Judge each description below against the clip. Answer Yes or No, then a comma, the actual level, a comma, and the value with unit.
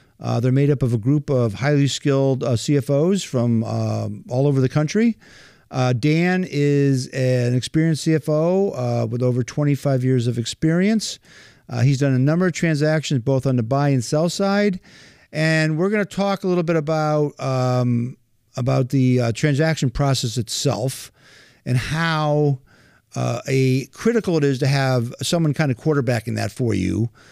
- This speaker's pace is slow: No, average, 170 wpm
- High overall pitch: No, medium, 140 Hz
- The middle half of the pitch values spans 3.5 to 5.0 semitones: Yes, average, 3.8 semitones